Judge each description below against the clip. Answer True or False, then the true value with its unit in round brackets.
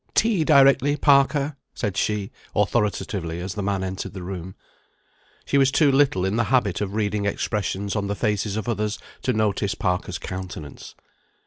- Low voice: True (105 Hz)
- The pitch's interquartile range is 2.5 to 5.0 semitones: False (5.4 semitones)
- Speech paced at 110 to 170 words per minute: True (160 wpm)